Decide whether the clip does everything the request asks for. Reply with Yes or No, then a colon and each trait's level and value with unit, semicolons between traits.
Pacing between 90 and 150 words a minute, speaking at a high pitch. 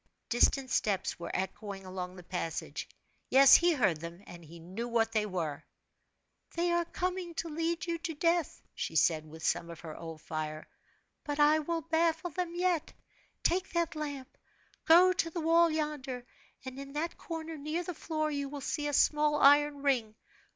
No: average, 175 wpm; very high, 290 Hz